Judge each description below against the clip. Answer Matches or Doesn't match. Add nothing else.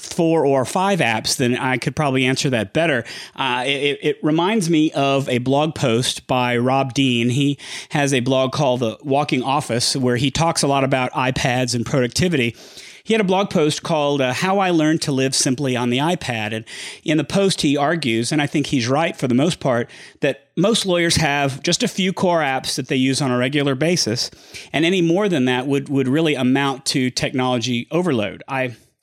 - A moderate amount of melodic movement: Matches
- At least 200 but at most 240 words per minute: Matches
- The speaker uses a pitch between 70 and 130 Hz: Doesn't match